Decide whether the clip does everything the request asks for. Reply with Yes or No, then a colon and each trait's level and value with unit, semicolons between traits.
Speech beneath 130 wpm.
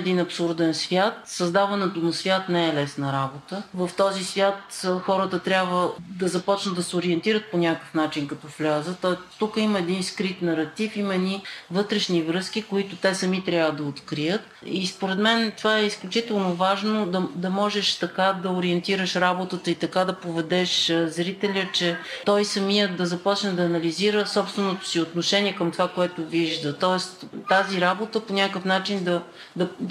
No: fast, 165 wpm